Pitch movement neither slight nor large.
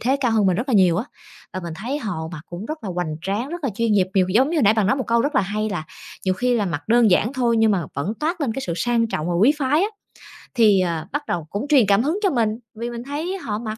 No: wide, 5.7 semitones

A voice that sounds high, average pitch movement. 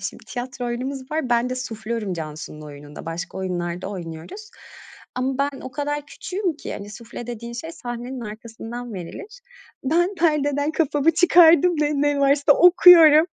No: very high, 255 Hz; wide, 5.8 semitones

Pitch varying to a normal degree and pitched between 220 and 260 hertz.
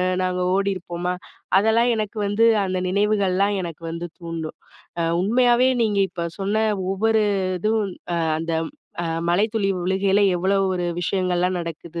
No: average, 3.2 semitones; high, 195 Hz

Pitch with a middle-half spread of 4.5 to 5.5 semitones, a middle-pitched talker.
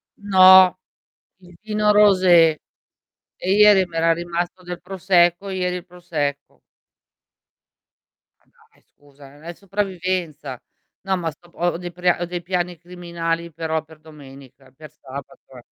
No: narrow, 2.6 semitones; medium, 175 Hz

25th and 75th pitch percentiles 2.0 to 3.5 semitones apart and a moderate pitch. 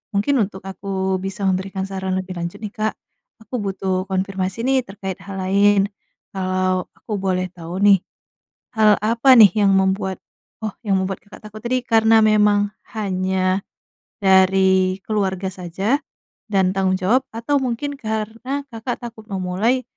No: narrow, 2.4 semitones; high, 195 Hz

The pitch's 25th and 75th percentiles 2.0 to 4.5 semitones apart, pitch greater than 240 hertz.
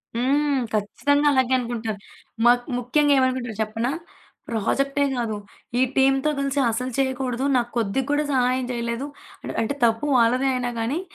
Yes: narrow, 2.6 semitones; very high, 250 Hz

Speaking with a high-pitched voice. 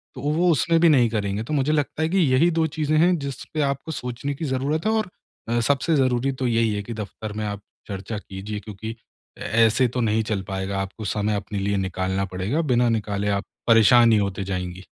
No: low, 115 Hz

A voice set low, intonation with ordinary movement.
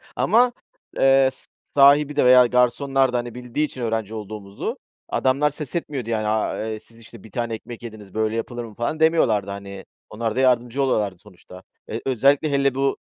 Yes: low, 120 Hz; average, 3.8 semitones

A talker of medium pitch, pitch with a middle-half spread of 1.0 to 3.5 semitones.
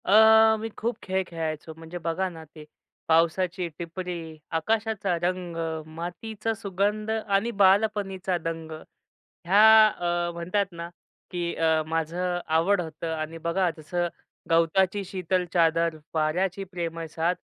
Yes: medium, 175 Hz; average, 2.8 semitones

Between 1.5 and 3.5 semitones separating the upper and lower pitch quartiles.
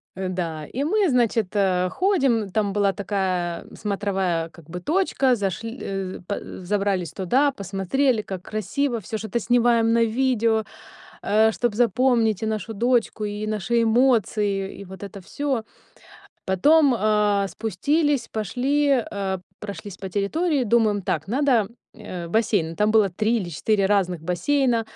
No: average, 3.9 semitones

